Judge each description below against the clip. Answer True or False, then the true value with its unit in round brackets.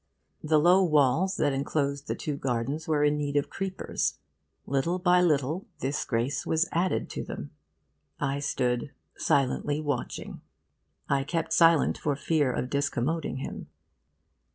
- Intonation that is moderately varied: True (3.0 semitones)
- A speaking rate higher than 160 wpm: False (140 wpm)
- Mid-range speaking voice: True (145 Hz)